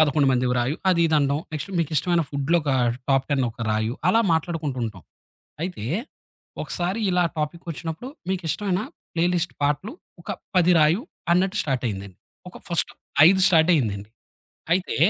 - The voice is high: No, medium, 155 Hz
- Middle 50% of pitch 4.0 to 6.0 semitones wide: Yes, average, 4.7 semitones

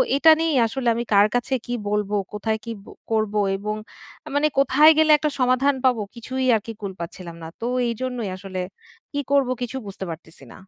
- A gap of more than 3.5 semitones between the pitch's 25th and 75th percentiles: Yes, average, 4.6 semitones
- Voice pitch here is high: Yes, high, 235 Hz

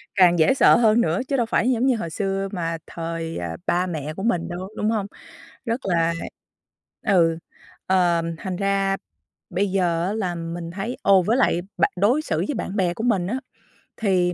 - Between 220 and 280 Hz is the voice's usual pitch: No, medium, 185 Hz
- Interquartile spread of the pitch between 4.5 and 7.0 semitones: No, average, 3.9 semitones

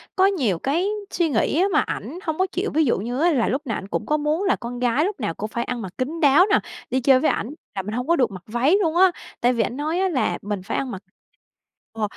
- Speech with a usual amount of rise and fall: No, wide, 6.2 semitones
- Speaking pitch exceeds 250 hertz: Yes, very high, 265 Hz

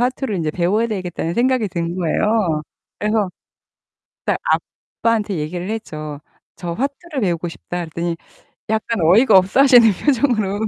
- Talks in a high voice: Yes, high, 200 Hz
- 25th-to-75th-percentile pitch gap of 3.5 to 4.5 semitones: No, average, 5.1 semitones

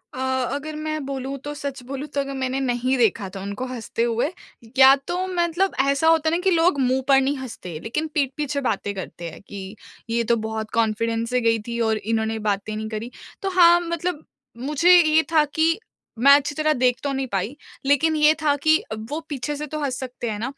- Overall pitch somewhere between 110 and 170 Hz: No, very high, 270 Hz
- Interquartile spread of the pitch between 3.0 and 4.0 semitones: No, average, 4.9 semitones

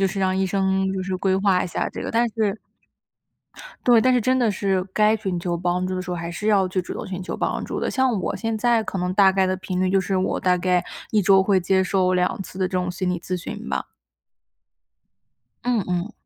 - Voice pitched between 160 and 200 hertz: Yes, high, 190 Hz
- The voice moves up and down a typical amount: No, narrow, 2.1 semitones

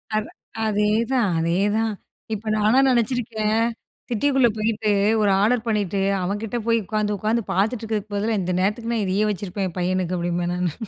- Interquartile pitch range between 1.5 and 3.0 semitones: Yes, narrow, 2.6 semitones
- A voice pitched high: Yes, high, 210 Hz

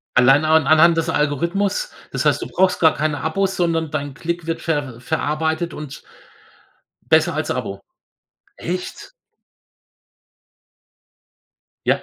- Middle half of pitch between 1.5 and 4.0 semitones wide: Yes, average, 2.7 semitones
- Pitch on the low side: No, medium, 160 Hz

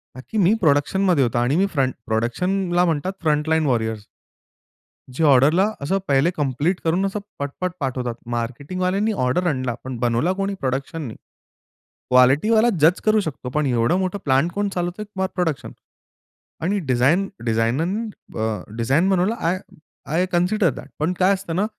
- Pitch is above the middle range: No, medium, 160 Hz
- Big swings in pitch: Yes, wide, 6.2 semitones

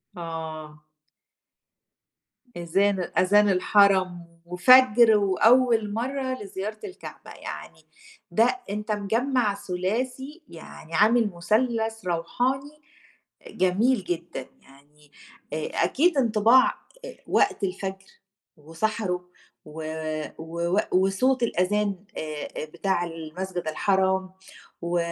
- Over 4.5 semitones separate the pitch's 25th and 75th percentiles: Yes, average, 4.9 semitones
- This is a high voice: Yes, high, 195 Hz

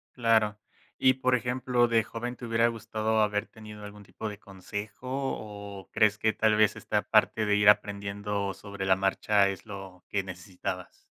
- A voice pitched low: Yes, low, 105 Hz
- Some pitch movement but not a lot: No, narrow, 2.1 semitones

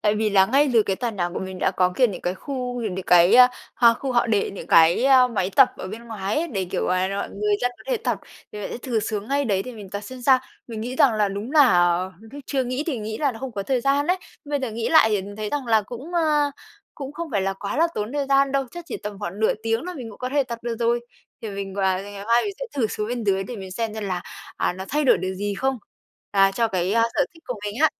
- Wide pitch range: No, average, 4.8 semitones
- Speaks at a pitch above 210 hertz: Yes, high, 225 Hz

